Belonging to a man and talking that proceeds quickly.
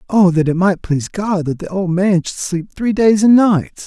Yes: male; fast, 250 wpm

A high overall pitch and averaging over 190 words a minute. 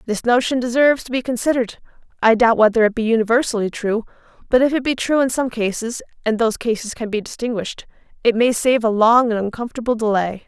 Yes: high, 230 Hz; average, 200 wpm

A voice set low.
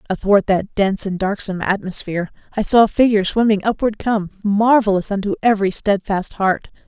No: high, 200 Hz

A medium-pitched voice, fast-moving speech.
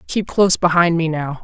Yes: medium, 170 Hz; fast, 210 wpm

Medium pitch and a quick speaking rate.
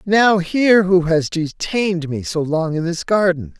No: medium, 180 Hz; average, 185 wpm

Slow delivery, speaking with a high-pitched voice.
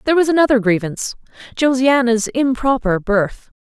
Yes: slow, 115 wpm; high, 245 Hz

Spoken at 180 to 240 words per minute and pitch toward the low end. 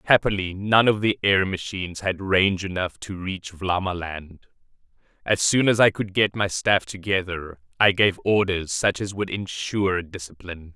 No: average, 160 wpm; very low, 95 Hz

